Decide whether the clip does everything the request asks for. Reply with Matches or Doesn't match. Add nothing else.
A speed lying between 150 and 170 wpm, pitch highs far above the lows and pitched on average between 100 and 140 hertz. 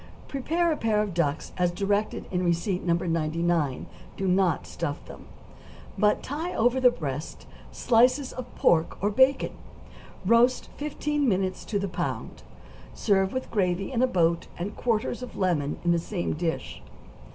Doesn't match